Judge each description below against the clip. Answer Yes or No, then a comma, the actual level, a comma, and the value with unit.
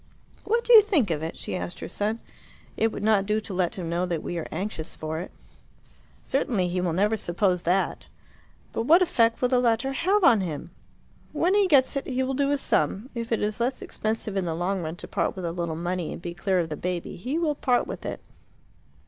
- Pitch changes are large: Yes, wide, 6.9 semitones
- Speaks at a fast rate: Yes, fast, 235 wpm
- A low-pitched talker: No, high, 210 Hz